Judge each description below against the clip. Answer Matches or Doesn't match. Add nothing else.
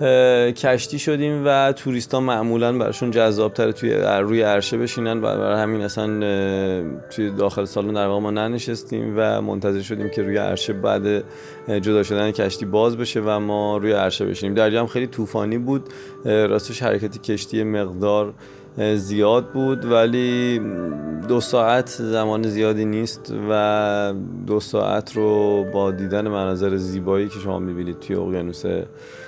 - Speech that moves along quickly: Doesn't match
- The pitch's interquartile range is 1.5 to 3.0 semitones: Matches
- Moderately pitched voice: Doesn't match